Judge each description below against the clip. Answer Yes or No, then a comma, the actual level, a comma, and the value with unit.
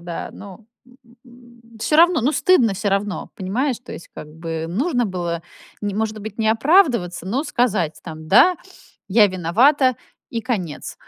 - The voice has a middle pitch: No, high, 215 Hz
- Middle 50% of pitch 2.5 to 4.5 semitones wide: No, wide, 5.6 semitones